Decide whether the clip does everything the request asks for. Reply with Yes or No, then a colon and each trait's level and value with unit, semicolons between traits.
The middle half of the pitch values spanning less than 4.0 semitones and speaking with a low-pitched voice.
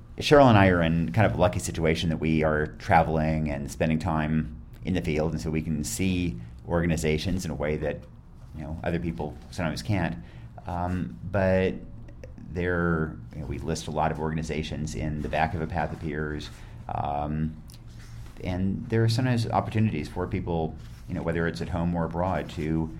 Yes: average, 2.7 semitones; very low, 80 Hz